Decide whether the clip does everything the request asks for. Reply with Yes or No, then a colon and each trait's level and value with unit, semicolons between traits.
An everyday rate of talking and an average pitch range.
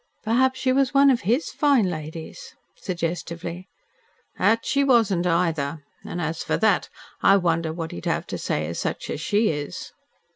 No: average, 170 wpm; wide, 6.9 semitones